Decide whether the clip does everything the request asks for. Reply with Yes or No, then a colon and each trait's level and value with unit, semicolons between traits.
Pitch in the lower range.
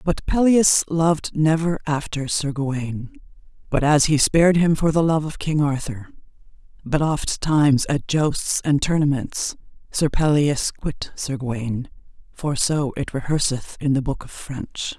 No: medium, 150 Hz